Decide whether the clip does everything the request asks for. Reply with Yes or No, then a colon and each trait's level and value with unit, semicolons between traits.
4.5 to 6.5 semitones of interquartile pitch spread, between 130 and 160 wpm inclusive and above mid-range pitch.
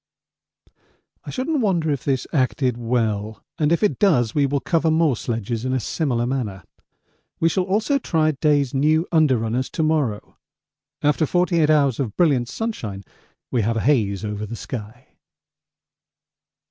No: wide, 5.6 semitones; average, 155 wpm; low, 135 Hz